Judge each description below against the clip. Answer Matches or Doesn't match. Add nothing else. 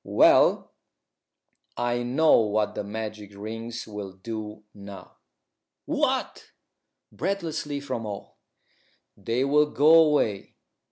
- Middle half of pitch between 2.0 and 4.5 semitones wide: Doesn't match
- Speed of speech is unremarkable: Doesn't match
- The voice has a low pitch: Matches